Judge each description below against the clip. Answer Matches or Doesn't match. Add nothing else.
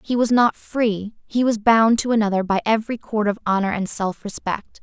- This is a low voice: Doesn't match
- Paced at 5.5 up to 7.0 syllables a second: Doesn't match